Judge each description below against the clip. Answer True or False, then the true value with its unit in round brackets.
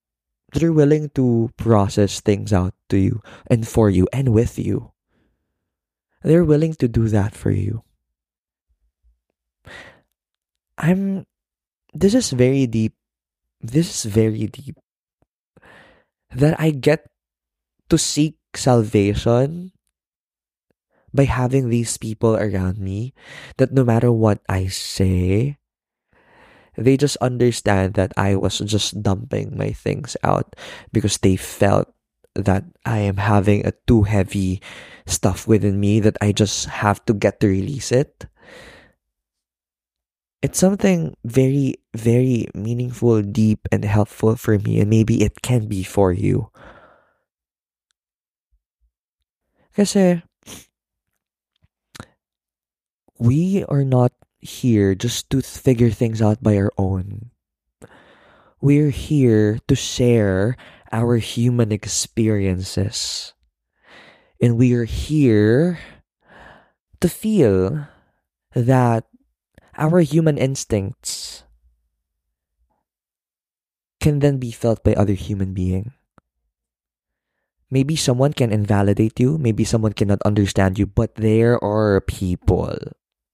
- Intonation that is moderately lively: True (4.8 semitones)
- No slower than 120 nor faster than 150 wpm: False (110 wpm)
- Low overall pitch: True (110 Hz)